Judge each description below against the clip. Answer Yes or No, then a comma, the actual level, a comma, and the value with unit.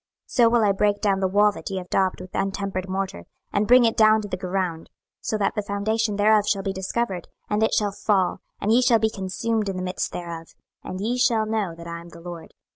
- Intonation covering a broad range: No, average, 2.7 semitones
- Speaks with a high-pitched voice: Yes, high, 200 Hz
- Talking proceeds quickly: Yes, fast, 245 wpm